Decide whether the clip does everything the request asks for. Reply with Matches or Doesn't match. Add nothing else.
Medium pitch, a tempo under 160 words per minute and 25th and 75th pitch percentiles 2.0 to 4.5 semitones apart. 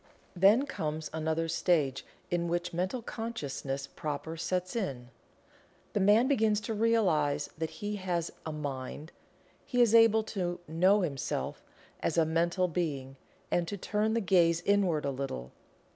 Doesn't match